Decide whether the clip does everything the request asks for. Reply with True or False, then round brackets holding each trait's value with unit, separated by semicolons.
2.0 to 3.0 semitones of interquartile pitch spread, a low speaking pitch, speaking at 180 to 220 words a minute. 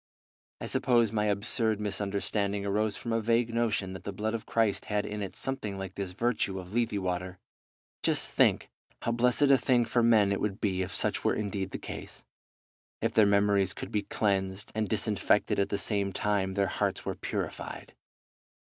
True (2.5 semitones; 105 Hz; 185 wpm)